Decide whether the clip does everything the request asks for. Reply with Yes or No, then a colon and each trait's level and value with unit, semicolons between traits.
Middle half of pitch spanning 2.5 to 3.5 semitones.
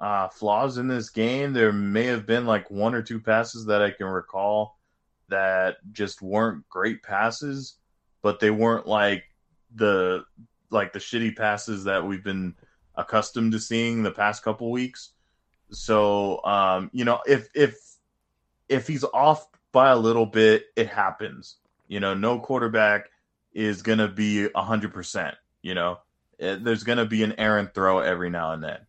Yes: average, 2.9 semitones